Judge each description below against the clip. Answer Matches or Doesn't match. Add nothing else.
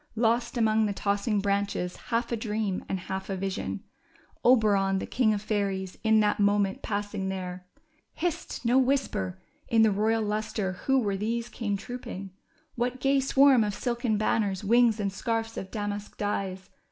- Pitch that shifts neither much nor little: Matches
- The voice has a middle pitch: Doesn't match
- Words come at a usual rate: Matches